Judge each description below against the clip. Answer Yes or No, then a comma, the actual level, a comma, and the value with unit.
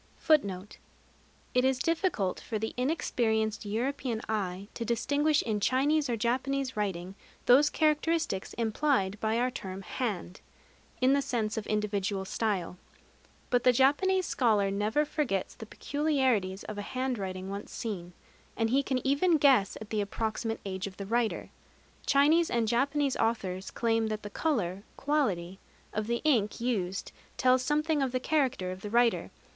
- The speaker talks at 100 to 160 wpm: Yes, average, 150 wpm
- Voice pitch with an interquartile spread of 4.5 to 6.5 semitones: Yes, average, 5.1 semitones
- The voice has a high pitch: Yes, high, 230 Hz